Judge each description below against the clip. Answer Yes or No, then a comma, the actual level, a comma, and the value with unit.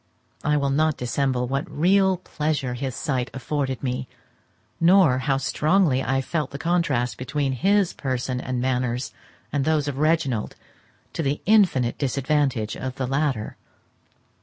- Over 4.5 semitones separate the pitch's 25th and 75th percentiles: No, average, 3.3 semitones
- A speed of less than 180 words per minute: Yes, average, 140 wpm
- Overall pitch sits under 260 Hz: Yes, medium, 140 Hz